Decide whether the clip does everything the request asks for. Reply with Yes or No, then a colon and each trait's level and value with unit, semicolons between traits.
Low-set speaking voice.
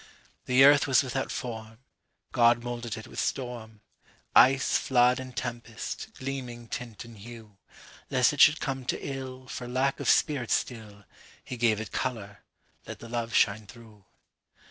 Yes: low, 120 Hz